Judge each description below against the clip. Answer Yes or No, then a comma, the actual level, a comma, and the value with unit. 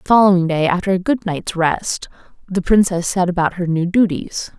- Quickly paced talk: No, average, 195 wpm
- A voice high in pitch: No, medium, 180 Hz